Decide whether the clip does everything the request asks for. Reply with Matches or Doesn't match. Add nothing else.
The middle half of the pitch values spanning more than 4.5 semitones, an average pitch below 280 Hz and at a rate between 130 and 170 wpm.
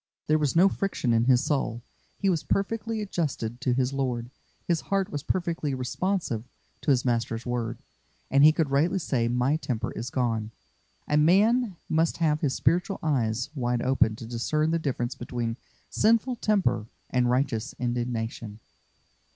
Matches